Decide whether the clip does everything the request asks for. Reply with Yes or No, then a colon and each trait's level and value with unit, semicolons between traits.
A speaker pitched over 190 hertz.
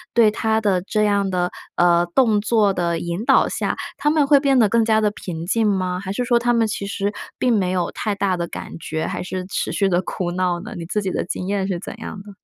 Yes: high, 200 Hz